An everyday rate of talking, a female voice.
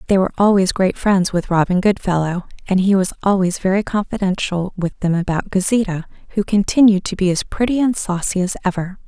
Yes: average, 185 wpm; female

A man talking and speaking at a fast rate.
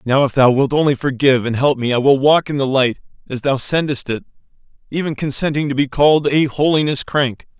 Yes: male; fast, 215 wpm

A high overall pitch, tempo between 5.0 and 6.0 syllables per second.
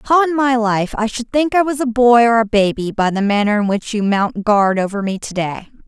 Yes: high, 225 Hz; 5.2 syllables/s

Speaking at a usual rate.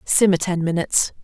Yes: average, 145 wpm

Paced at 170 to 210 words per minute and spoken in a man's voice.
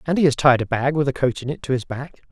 No: fast, 365 wpm; male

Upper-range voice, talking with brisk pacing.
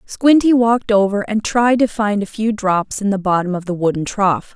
Yes: high, 210 Hz; fast, 225 wpm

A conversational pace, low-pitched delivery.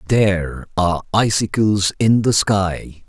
No: slow, 115 wpm; low, 100 Hz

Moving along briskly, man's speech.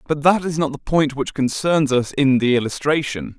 Yes: fast, 215 wpm; male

